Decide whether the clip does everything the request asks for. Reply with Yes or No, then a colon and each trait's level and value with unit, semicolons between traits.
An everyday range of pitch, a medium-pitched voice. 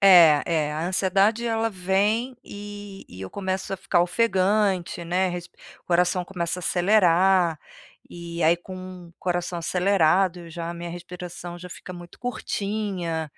No: narrow, 2.2 semitones; medium, 180 Hz